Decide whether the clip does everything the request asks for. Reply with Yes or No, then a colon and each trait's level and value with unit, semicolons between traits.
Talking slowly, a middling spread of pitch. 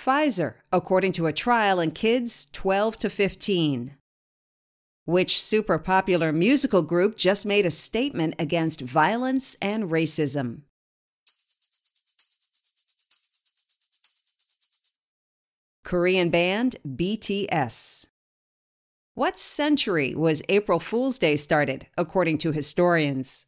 Yes: slow, 90 wpm; average, 4.8 semitones